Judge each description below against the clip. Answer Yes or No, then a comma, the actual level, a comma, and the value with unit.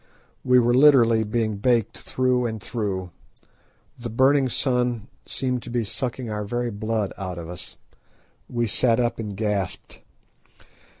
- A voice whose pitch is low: Yes, low, 115 Hz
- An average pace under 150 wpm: Yes, average, 140 wpm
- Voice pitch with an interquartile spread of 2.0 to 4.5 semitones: Yes, average, 2.9 semitones